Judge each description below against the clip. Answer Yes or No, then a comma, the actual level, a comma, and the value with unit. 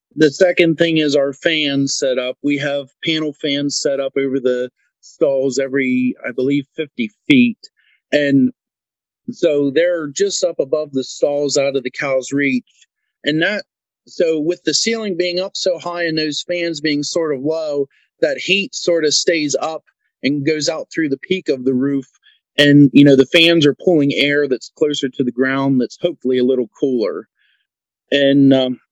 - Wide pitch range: No, average, 3.9 semitones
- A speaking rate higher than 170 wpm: Yes, average, 180 wpm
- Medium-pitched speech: Yes, medium, 145 Hz